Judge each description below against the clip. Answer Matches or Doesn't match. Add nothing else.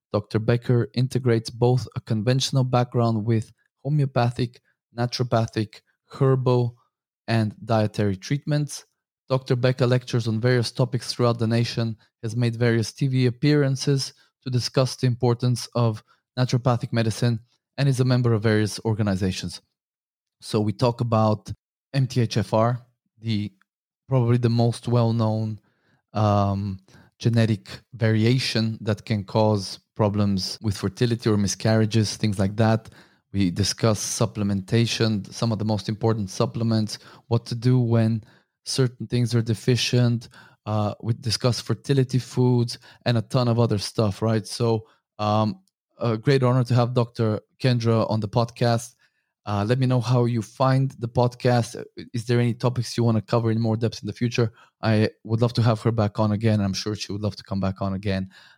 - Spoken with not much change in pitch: Matches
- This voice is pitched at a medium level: Doesn't match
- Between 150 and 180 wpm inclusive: Matches